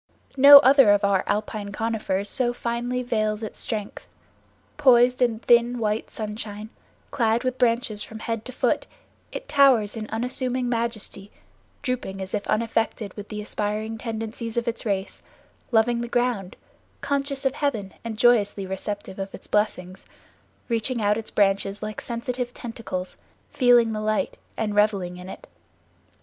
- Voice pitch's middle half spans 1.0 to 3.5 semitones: Yes, average, 2.7 semitones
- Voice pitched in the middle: No, high, 225 Hz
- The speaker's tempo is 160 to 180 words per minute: No, average, 150 wpm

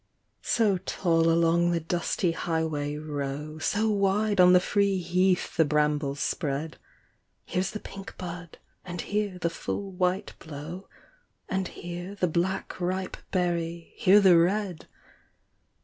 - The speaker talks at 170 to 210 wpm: No, slow, 135 wpm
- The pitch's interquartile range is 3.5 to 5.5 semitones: No, average, 2.7 semitones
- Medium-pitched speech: Yes, medium, 175 Hz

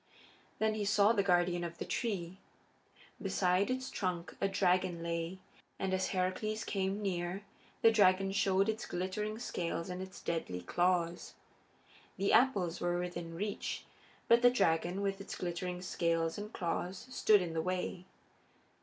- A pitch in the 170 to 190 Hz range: Yes, medium, 185 Hz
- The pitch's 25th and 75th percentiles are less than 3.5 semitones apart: Yes, narrow, 2.5 semitones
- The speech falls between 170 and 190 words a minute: No, average, 150 wpm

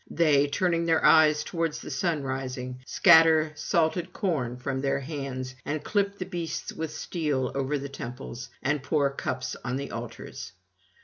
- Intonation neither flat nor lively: Yes, average, 3.5 semitones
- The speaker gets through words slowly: No, average, 150 wpm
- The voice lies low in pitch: No, medium, 145 Hz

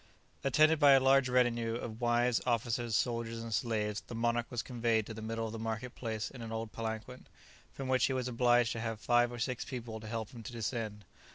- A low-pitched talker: Yes, low, 115 Hz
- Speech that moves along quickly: Yes, fast, 220 wpm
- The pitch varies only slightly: Yes, narrow, 1.7 semitones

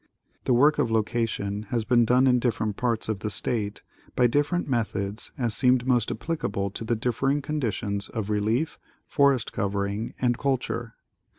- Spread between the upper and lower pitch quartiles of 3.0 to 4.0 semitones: Yes, average, 3.3 semitones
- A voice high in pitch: No, low, 115 Hz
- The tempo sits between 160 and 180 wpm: Yes, average, 165 wpm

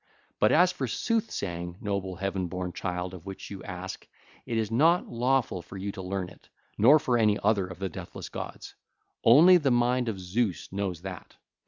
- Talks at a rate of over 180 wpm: Yes, average, 190 wpm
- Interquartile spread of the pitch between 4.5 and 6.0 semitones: Yes, average, 4.8 semitones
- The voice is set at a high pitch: No, low, 100 Hz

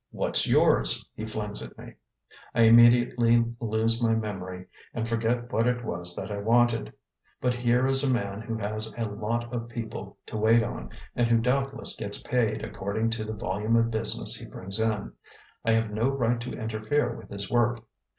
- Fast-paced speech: No, average, 185 wpm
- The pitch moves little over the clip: Yes, narrow, 1.8 semitones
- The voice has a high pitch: No, low, 115 Hz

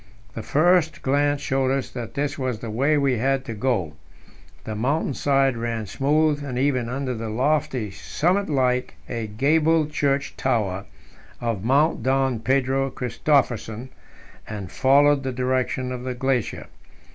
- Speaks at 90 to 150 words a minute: Yes, average, 145 wpm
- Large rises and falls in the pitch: No, average, 3.1 semitones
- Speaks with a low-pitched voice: Yes, low, 130 Hz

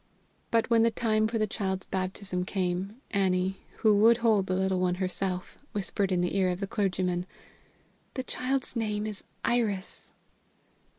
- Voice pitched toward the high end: Yes, high, 195 Hz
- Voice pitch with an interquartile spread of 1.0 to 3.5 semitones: Yes, average, 2.9 semitones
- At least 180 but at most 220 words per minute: No, average, 160 wpm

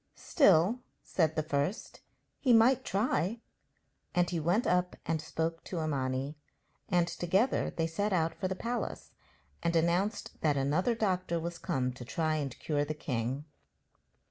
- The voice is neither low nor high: Yes, medium, 170 Hz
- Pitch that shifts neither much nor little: Yes, average, 3.8 semitones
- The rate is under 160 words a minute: Yes, average, 150 wpm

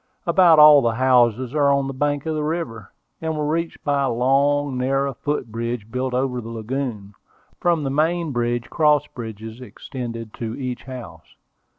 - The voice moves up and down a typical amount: Yes, average, 3.8 semitones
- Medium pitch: No, low, 130 Hz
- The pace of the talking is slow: No, average, 175 wpm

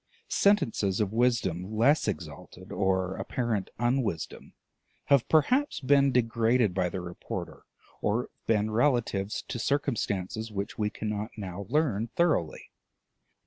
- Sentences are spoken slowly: Yes, slow, 125 wpm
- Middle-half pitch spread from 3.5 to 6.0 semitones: Yes, average, 4.6 semitones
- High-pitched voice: No, low, 110 Hz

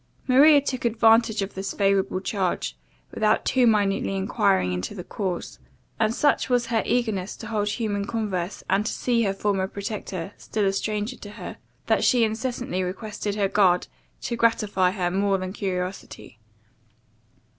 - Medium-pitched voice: No, high, 205 Hz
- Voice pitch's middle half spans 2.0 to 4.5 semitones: Yes, average, 2.8 semitones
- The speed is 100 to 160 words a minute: Yes, average, 155 wpm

